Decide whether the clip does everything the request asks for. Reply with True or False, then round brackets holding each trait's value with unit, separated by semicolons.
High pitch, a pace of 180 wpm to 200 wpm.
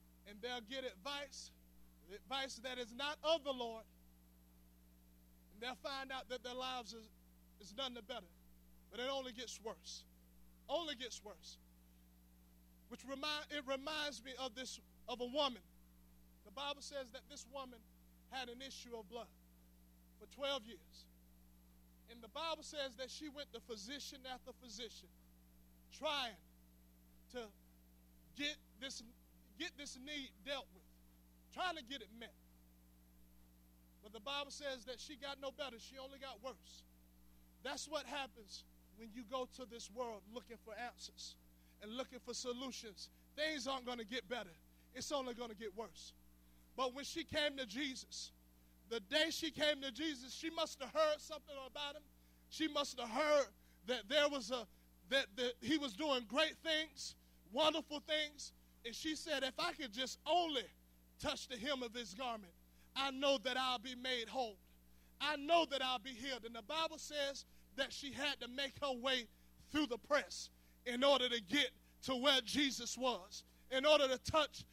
False (245 Hz; 165 wpm)